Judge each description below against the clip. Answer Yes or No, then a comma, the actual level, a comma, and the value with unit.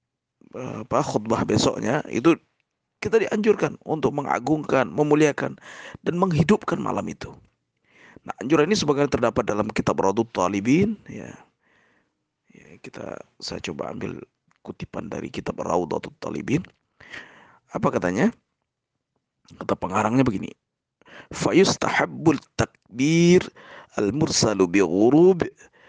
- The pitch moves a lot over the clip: Yes, wide, 8.5 semitones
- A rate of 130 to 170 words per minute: No, average, 100 wpm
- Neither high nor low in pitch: Yes, medium, 150 Hz